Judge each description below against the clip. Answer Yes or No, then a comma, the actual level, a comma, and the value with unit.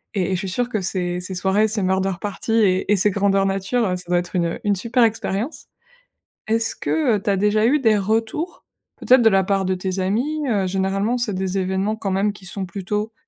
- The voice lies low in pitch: No, high, 200 Hz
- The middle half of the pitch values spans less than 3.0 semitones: Yes, narrow, 2.6 semitones